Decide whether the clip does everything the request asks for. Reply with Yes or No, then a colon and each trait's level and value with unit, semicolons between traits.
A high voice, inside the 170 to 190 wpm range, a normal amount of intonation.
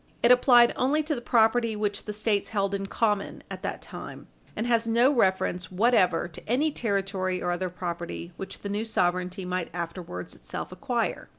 Yes: high, 200 Hz; average, 180 wpm; average, 4.3 semitones